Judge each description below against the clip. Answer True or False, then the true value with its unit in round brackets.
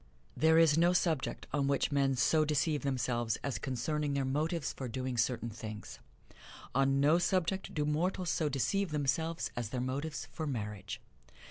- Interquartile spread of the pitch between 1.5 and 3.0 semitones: False (3.8 semitones)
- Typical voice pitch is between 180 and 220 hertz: False (140 Hz)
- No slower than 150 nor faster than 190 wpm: True (160 wpm)